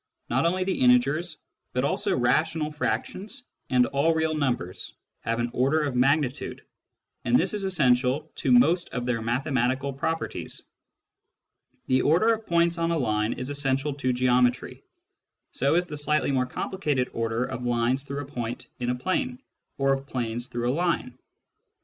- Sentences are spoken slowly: No, average, 165 wpm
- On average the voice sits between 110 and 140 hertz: Yes, low, 135 Hz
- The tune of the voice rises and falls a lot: No, average, 4.3 semitones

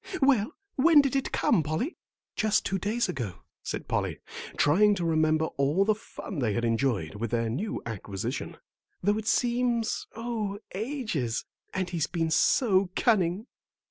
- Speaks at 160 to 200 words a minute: No, average, 150 wpm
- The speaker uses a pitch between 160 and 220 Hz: Yes, high, 190 Hz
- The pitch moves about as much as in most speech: No, wide, 8.4 semitones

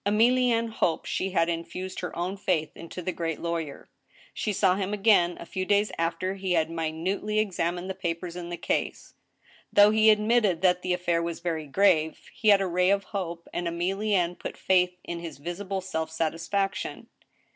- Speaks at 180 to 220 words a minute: Yes, average, 185 wpm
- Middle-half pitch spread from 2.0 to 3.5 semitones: Yes, average, 2.9 semitones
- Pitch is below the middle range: No, medium, 180 Hz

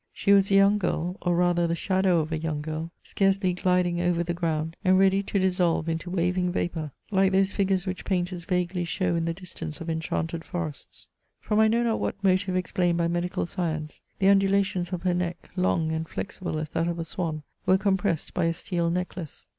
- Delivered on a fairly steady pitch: Yes, narrow, 2.2 semitones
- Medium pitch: Yes, medium, 180 Hz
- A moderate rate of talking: No, fast, 210 wpm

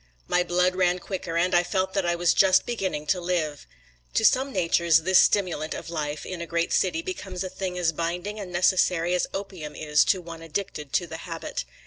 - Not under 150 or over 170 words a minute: No, fast, 205 wpm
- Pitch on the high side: No, medium, 180 Hz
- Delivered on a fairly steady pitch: Yes, narrow, 2.1 semitones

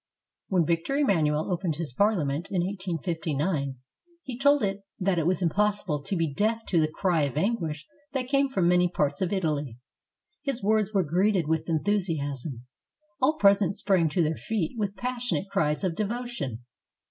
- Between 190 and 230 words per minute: No, average, 165 wpm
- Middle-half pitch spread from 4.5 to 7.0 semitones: Yes, average, 5.0 semitones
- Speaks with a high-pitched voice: No, medium, 180 Hz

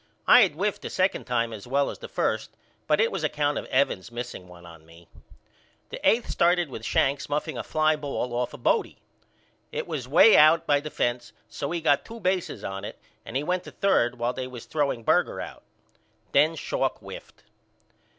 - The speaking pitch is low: No, medium, 145 Hz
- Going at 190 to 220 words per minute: Yes, average, 200 wpm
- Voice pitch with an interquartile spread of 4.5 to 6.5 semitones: Yes, wide, 5.6 semitones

